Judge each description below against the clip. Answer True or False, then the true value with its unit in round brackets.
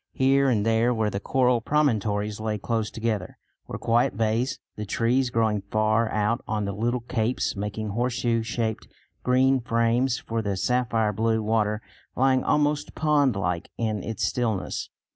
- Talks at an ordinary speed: True (155 wpm)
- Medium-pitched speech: False (115 Hz)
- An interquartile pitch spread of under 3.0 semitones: True (2.6 semitones)